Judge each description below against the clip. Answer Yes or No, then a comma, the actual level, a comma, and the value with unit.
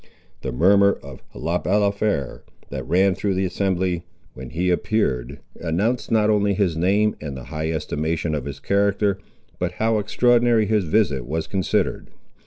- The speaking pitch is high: No, very low, 95 Hz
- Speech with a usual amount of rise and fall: Yes, average, 4.6 semitones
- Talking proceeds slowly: No, average, 155 wpm